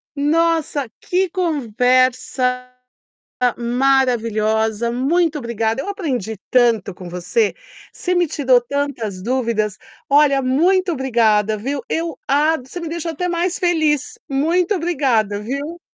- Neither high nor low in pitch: No, very high, 270 Hz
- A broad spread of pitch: Yes, wide, 6.0 semitones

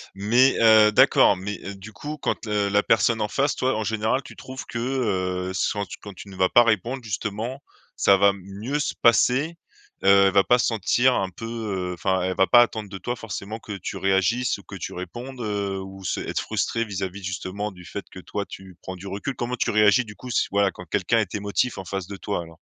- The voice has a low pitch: Yes, low, 105 Hz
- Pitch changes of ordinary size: Yes, average, 3.3 semitones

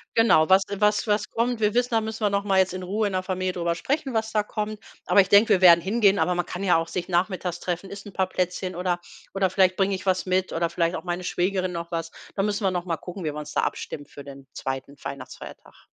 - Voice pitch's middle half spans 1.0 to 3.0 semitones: Yes, average, 2.7 semitones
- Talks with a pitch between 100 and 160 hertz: No, medium, 185 Hz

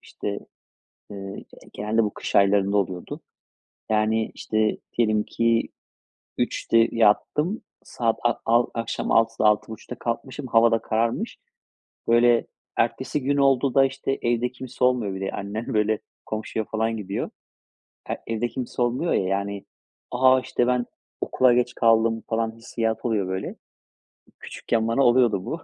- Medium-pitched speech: No, low, 115 Hz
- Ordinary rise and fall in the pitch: No, narrow, 2.3 semitones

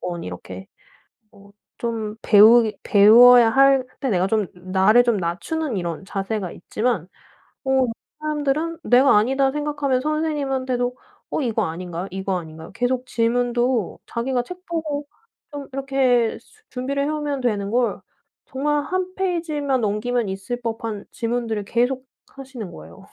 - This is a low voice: No, high, 245 Hz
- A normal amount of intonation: Yes, average, 4.8 semitones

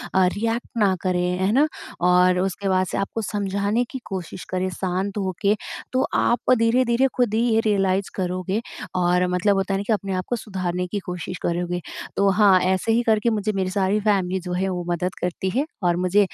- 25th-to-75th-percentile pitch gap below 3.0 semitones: Yes, narrow, 2.5 semitones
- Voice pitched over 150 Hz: Yes, high, 190 Hz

